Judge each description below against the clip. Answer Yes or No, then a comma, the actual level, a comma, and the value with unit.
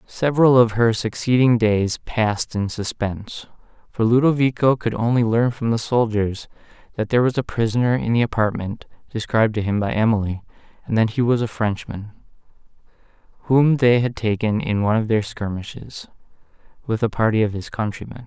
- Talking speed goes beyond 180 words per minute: No, average, 165 wpm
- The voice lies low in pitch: Yes, low, 115 Hz